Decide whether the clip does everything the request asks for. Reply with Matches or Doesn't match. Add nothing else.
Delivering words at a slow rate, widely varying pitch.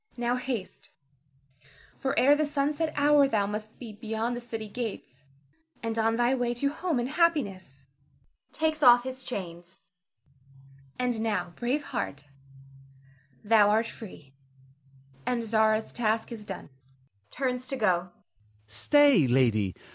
Doesn't match